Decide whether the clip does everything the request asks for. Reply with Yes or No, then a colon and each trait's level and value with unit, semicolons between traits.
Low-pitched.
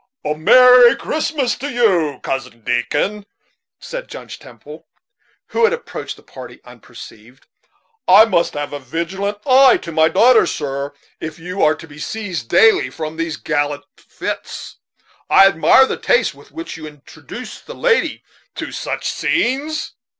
No: medium, 185 Hz